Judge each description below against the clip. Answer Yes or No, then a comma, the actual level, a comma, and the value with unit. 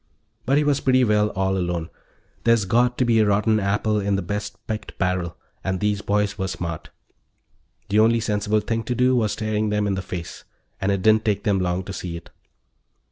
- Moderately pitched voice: No, low, 105 Hz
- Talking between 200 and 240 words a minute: Yes, fast, 205 wpm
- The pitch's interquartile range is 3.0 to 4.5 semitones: No, narrow, 2.5 semitones